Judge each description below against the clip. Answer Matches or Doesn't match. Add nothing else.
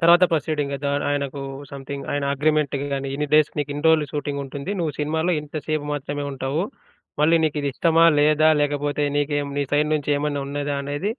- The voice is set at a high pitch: Doesn't match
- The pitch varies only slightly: Matches